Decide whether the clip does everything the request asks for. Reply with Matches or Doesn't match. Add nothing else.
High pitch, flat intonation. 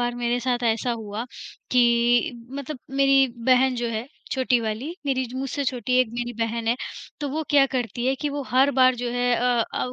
Matches